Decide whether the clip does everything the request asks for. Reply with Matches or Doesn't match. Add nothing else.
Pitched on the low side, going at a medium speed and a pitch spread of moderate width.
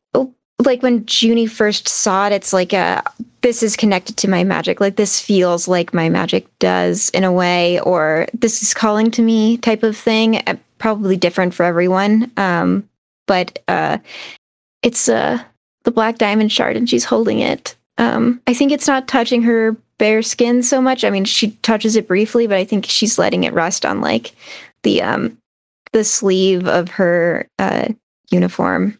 Doesn't match